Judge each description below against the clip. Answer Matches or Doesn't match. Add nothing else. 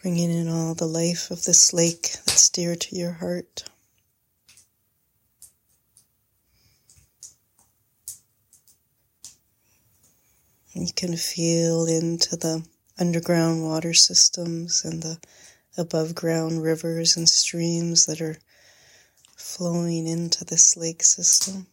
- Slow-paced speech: Matches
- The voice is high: Doesn't match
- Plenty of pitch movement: Matches